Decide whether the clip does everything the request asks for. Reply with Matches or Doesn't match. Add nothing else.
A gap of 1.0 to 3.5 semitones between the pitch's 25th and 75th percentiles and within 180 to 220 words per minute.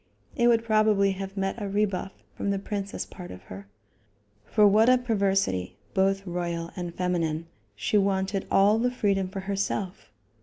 Doesn't match